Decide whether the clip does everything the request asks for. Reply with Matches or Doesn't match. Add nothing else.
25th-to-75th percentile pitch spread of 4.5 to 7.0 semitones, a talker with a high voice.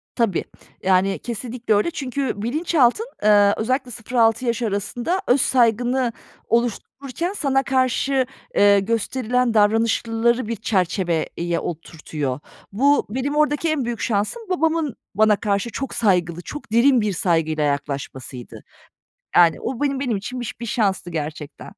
Matches